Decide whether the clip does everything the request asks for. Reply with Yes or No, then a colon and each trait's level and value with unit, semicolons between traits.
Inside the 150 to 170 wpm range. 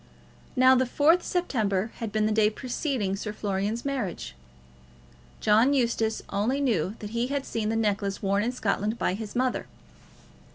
Yes: average, 160 wpm